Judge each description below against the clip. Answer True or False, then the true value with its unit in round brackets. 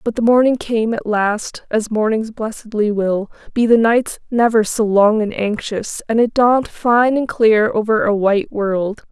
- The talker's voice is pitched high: True (220 Hz)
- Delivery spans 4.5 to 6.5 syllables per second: False (4.3 syllables/s)